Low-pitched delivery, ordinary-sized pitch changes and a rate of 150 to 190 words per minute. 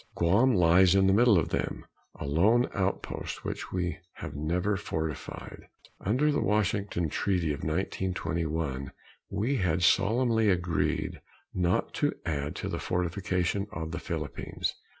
No: very low, 90 Hz; average, 3.6 semitones; slow, 135 wpm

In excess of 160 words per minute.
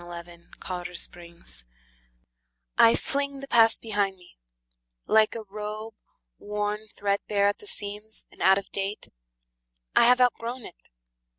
No: average, 140 wpm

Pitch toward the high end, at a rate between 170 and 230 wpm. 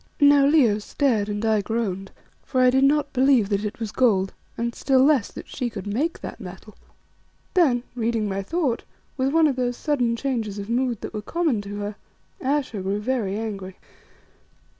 Yes: high, 235 Hz; average, 180 wpm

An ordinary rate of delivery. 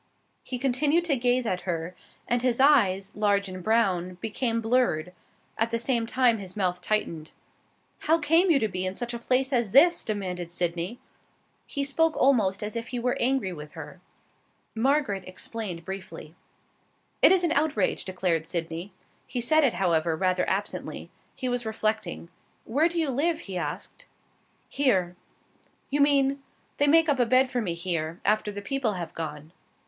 Yes: average, 170 wpm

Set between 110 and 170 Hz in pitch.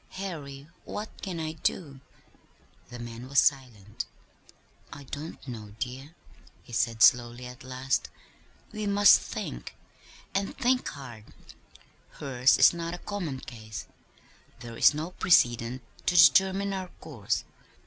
Yes: low, 135 Hz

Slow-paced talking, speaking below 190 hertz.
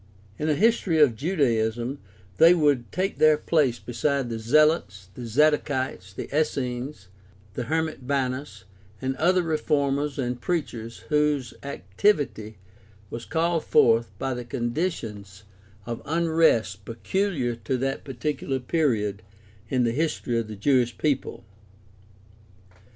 Yes: slow, 125 wpm; low, 135 Hz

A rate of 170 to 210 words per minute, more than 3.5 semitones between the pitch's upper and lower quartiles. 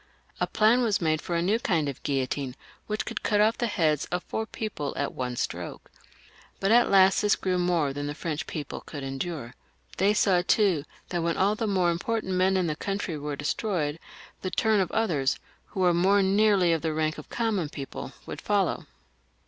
Yes: average, 200 wpm; average, 5.2 semitones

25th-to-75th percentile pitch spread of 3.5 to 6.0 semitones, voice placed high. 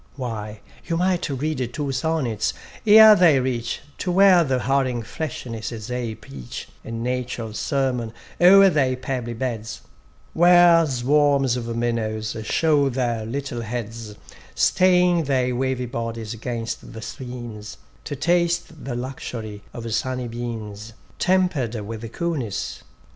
No: average, 4.4 semitones; low, 125 Hz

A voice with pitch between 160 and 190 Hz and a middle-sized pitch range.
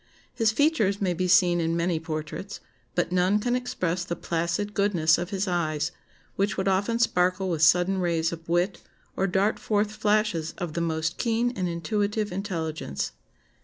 Yes: medium, 185 Hz; average, 3.4 semitones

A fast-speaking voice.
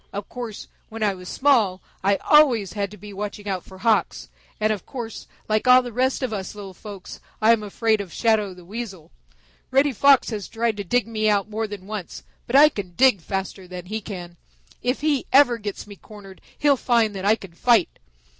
Yes: fast, 210 wpm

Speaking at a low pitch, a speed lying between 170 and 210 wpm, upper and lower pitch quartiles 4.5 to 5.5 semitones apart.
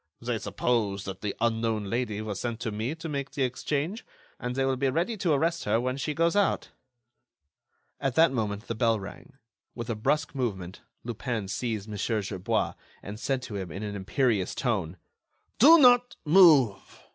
Yes: low, 120 Hz; average, 180 wpm; average, 5.2 semitones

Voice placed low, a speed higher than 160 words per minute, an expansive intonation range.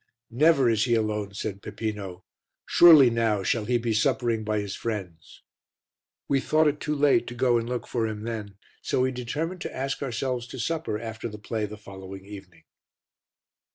No: low, 115 Hz; average, 180 wpm; average, 3.7 semitones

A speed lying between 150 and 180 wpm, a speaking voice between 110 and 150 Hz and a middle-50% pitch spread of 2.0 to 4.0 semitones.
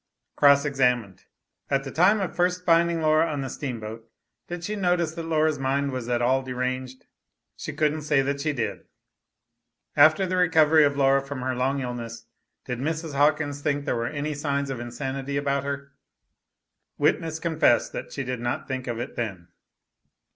Yes: average, 175 wpm; medium, 140 Hz; average, 3.5 semitones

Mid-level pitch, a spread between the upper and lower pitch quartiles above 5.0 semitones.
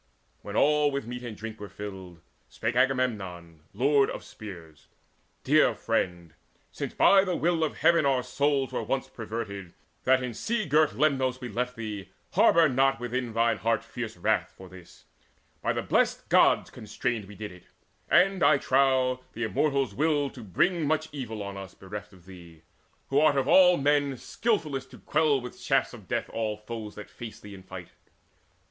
No: low, 125 Hz; wide, 5.5 semitones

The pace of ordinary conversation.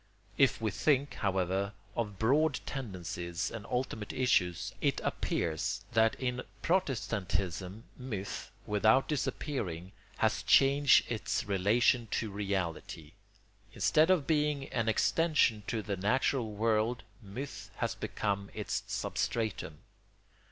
No: slow, 110 wpm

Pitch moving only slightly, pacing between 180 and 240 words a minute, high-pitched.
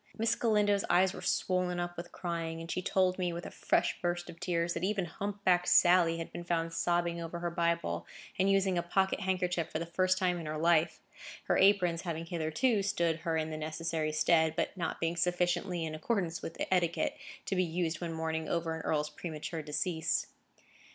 No: narrow, 1.9 semitones; average, 200 wpm; medium, 170 Hz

